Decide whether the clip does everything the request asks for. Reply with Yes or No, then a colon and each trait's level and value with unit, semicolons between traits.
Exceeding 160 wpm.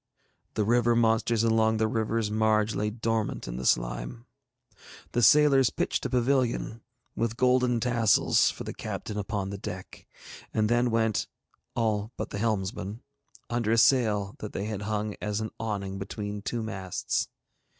No: average, 155 wpm